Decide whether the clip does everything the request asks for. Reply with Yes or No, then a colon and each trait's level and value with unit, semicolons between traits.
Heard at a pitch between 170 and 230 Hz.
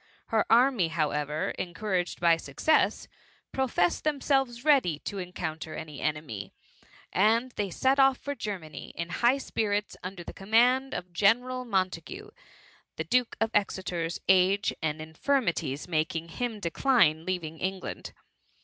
Yes: high, 190 Hz